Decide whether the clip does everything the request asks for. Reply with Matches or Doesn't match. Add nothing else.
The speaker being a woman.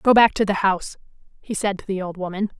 Matches